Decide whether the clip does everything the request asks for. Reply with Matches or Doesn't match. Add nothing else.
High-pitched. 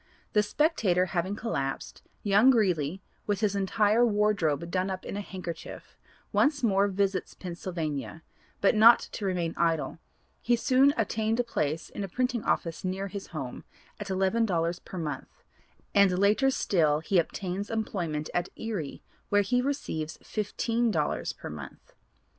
Matches